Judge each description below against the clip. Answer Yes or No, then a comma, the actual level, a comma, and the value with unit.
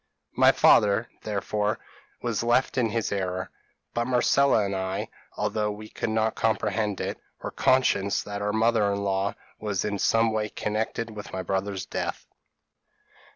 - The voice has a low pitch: Yes, low, 105 Hz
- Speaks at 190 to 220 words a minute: No, average, 155 wpm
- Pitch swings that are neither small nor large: No, narrow, 2.1 semitones